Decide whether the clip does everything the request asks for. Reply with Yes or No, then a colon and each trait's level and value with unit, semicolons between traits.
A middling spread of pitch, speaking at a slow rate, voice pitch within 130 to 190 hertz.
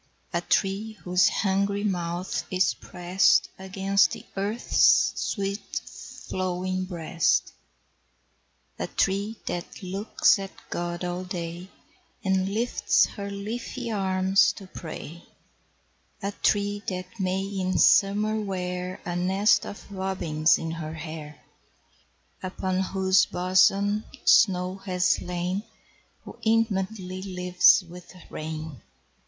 No: narrow, 1.8 semitones; slow, 110 wpm; medium, 185 Hz